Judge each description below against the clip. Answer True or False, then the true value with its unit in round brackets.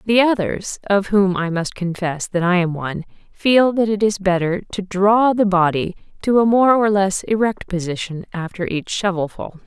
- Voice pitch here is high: True (195 Hz)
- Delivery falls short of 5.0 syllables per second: True (4.7 syllables/s)